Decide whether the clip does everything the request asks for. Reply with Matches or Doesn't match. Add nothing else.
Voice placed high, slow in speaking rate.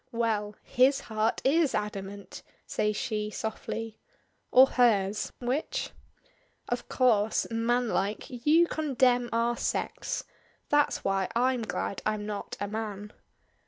Matches